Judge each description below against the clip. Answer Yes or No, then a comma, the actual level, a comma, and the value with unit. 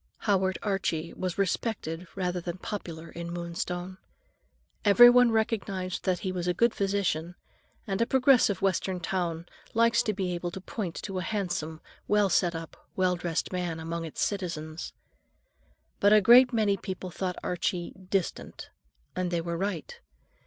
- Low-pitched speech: No, medium, 185 Hz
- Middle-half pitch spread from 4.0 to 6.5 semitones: No, average, 2.9 semitones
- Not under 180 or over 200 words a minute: No, average, 150 wpm